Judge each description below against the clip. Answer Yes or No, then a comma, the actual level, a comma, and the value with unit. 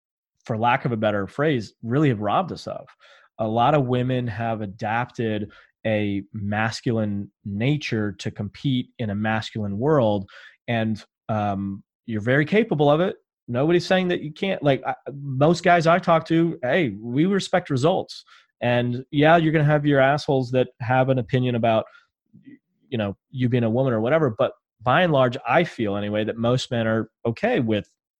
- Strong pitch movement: Yes, wide, 5.7 semitones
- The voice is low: Yes, low, 125 Hz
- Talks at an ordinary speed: Yes, average, 175 wpm